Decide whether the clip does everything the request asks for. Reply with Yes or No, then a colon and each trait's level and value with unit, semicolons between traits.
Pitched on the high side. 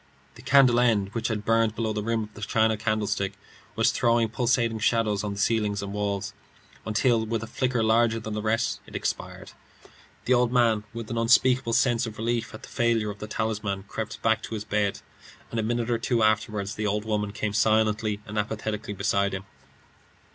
No: low, 110 Hz